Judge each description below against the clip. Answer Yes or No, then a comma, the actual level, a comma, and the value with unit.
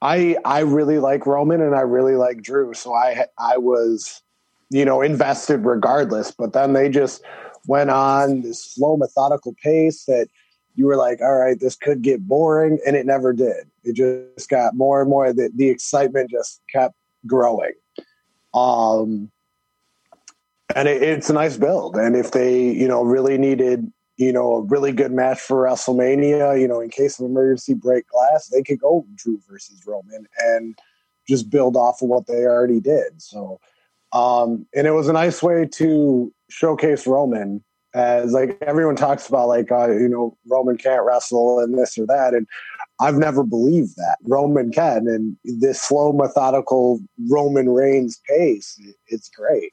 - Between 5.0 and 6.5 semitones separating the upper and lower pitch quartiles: No, narrow, 2.5 semitones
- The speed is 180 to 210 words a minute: No, average, 170 wpm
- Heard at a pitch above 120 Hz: Yes, low, 130 Hz